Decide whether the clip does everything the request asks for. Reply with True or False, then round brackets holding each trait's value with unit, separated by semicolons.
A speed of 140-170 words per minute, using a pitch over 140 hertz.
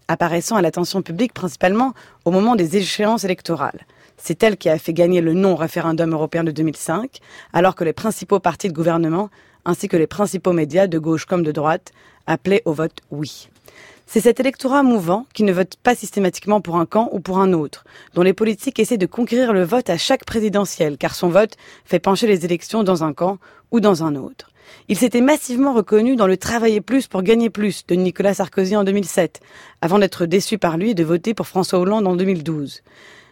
False (200 wpm; 185 Hz)